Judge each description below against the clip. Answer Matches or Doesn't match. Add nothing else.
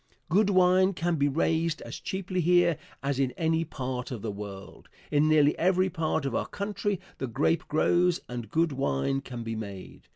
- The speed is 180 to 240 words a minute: Matches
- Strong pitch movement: Matches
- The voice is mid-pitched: Matches